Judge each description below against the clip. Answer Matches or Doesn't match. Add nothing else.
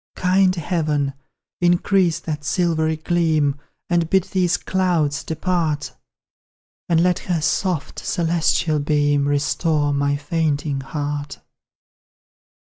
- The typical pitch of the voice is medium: Matches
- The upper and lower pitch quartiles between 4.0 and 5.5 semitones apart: Doesn't match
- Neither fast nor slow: Doesn't match